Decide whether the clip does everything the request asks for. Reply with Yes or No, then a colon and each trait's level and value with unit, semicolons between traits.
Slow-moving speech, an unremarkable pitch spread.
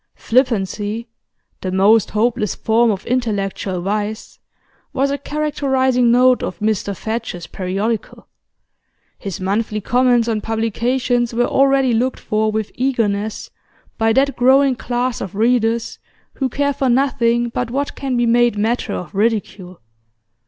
Yes: slow, 130 wpm; average, 3.1 semitones